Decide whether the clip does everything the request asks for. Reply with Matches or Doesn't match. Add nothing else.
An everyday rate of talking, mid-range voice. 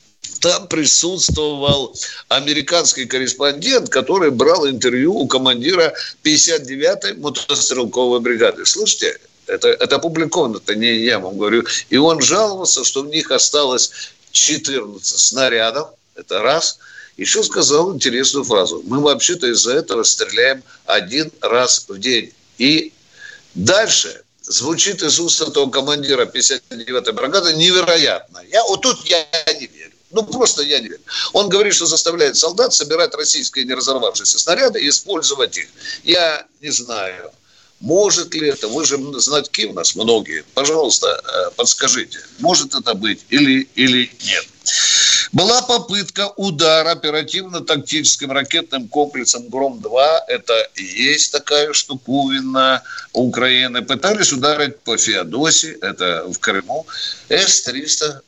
Matches